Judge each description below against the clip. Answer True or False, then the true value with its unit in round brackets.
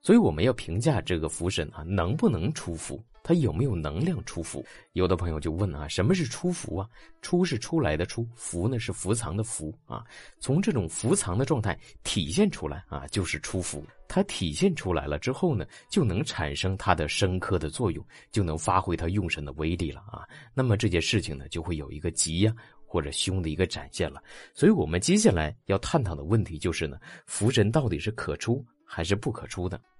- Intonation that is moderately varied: False (6.5 semitones)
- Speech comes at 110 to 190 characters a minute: False (310 characters per minute)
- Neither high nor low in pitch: False (95 Hz)